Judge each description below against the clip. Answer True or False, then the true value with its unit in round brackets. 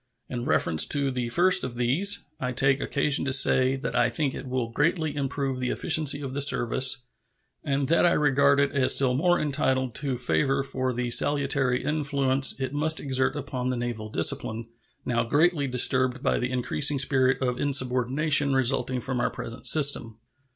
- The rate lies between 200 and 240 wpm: False (175 wpm)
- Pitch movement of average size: False (2.2 semitones)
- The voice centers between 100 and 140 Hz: True (135 Hz)